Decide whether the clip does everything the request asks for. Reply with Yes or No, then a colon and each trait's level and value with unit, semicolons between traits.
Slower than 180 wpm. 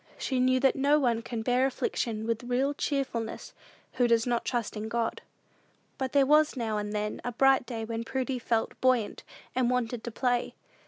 No: average, 195 wpm